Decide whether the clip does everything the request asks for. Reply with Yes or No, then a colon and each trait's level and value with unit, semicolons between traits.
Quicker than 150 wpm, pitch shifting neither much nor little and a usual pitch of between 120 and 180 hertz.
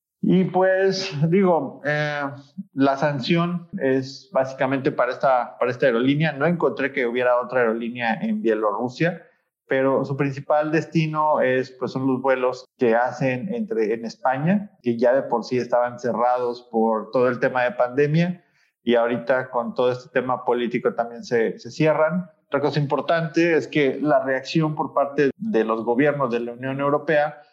Yes: average, 165 wpm; average, 4.3 semitones; medium, 140 Hz